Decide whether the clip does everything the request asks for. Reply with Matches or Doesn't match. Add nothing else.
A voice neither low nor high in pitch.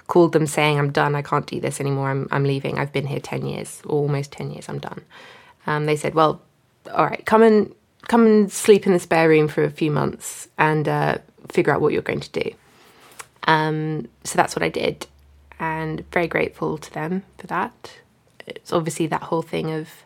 Matches